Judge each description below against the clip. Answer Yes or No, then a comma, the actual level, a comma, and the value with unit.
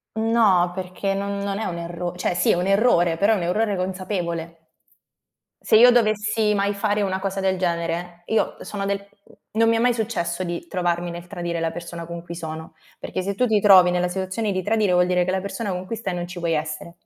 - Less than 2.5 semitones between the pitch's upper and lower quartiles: No, average, 2.8 semitones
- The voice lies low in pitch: No, medium, 185 Hz